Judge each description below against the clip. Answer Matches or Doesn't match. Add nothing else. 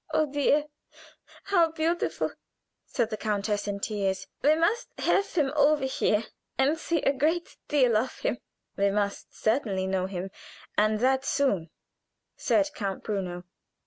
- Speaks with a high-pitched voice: Matches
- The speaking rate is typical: Matches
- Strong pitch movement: Matches